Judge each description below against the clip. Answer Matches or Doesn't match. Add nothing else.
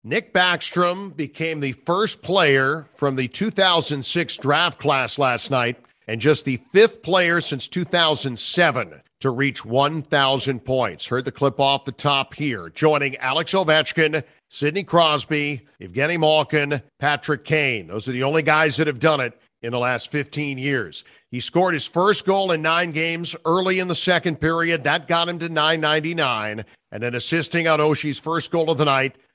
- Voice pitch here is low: Doesn't match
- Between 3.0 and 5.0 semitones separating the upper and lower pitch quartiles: Matches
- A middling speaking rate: Matches